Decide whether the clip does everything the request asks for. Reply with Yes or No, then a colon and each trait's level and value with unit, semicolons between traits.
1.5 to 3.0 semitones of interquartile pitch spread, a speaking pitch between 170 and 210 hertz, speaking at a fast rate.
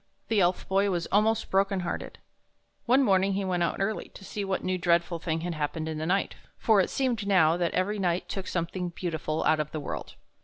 Yes: average, 2.7 semitones; medium, 185 Hz; fast, 225 wpm